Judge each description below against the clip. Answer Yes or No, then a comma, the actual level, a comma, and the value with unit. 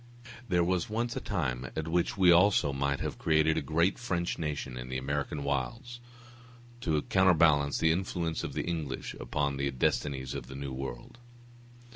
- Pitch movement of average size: Yes, average, 4.2 semitones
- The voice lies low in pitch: Yes, very low, 75 Hz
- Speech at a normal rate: Yes, average, 170 wpm